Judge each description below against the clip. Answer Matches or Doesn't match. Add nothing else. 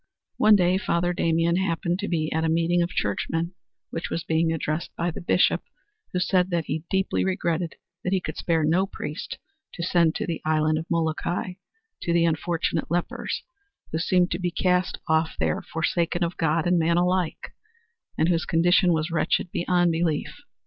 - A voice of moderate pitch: Matches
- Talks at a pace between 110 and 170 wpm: Doesn't match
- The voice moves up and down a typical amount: Doesn't match